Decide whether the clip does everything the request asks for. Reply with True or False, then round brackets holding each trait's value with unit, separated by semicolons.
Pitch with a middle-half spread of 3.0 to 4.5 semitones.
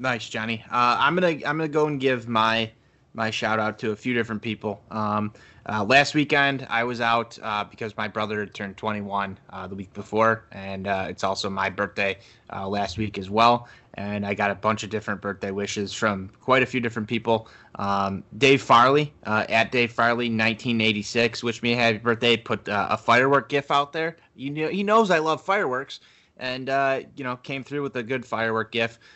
True (3.4 semitones)